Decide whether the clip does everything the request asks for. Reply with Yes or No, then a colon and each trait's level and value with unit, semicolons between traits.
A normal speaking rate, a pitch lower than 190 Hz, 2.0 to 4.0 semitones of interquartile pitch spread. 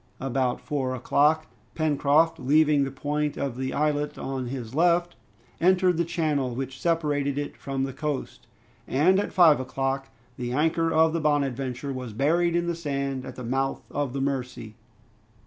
Yes: average, 165 wpm; medium, 140 Hz; average, 3.1 semitones